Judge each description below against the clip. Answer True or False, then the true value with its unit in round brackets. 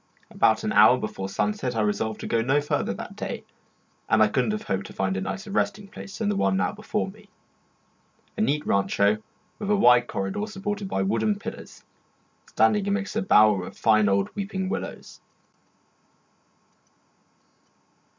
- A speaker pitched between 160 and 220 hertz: False (125 Hz)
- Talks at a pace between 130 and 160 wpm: False (170 wpm)